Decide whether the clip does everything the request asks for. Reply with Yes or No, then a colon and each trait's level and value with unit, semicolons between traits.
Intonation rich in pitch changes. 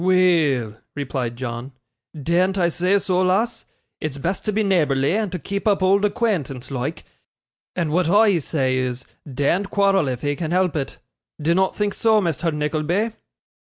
Yes: wide, 5.7 semitones